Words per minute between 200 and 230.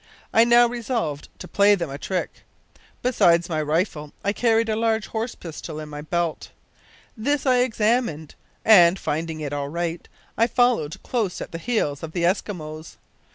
No: average, 165 wpm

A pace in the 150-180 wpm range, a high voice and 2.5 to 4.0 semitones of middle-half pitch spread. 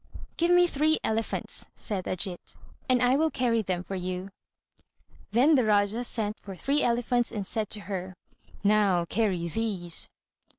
No: average, 155 wpm; high, 215 Hz; average, 4.7 semitones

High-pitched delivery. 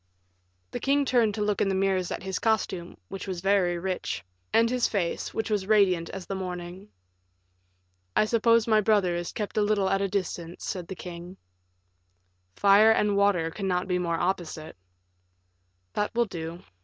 Yes: high, 195 Hz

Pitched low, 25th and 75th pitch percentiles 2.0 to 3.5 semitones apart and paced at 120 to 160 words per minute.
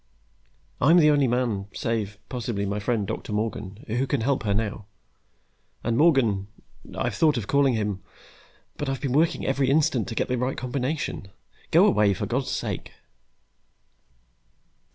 No: low, 120 Hz; average, 4.5 semitones; average, 155 wpm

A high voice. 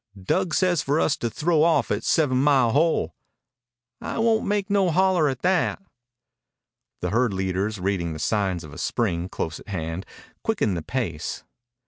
No: low, 125 Hz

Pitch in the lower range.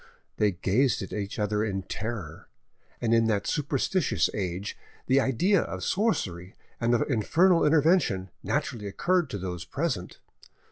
Yes: low, 110 Hz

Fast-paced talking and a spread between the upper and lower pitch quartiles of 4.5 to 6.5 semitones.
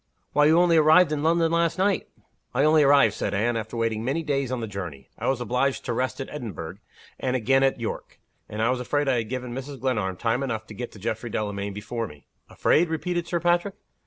Yes: fast, 225 wpm; wide, 5.4 semitones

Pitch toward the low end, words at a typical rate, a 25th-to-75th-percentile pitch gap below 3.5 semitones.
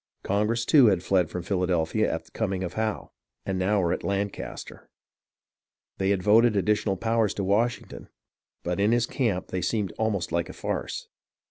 Yes: low, 100 Hz; average, 170 wpm; average, 3.1 semitones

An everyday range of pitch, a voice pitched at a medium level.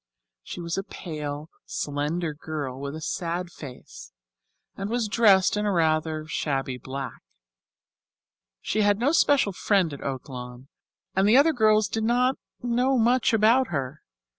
No: wide, 7.2 semitones; medium, 175 Hz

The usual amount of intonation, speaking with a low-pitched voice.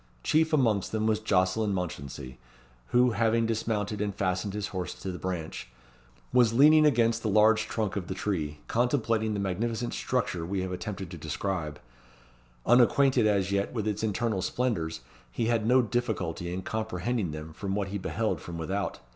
Yes: average, 3.8 semitones; low, 105 Hz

